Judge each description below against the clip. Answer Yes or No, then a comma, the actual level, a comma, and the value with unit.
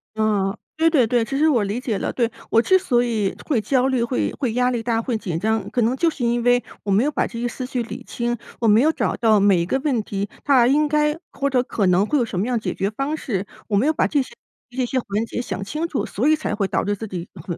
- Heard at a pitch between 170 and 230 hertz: No, high, 240 Hz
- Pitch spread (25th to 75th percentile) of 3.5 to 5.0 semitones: Yes, average, 4.1 semitones